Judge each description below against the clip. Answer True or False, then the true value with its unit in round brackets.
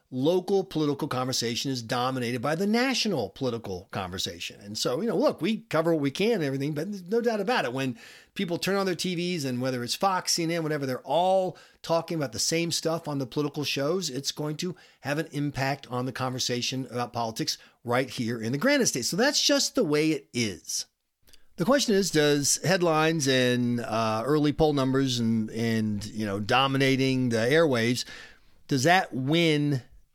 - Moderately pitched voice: True (145 Hz)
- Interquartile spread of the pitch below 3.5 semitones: False (5.4 semitones)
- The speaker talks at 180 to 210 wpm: True (190 wpm)